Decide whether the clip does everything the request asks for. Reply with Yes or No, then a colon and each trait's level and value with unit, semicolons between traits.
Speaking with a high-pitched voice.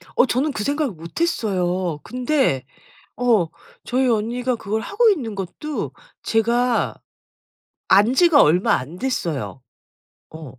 Yes: high, 230 Hz